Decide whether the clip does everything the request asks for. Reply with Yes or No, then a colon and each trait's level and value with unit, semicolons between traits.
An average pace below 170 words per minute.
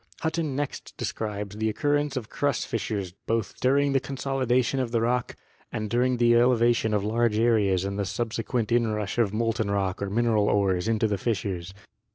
No: average, 185 wpm